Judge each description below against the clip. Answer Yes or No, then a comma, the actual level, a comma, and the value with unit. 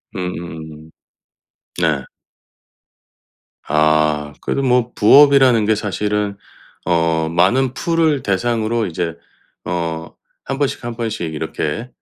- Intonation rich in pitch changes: Yes, wide, 6.9 semitones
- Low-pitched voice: Yes, low, 100 Hz